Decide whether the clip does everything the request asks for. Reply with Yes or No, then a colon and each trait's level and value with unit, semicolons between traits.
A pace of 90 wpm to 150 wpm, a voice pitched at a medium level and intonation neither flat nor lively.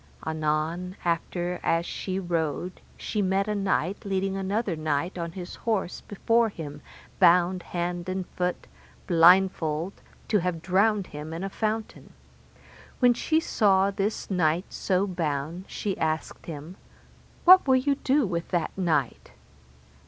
Yes: average, 140 wpm; medium, 180 Hz; average, 3.0 semitones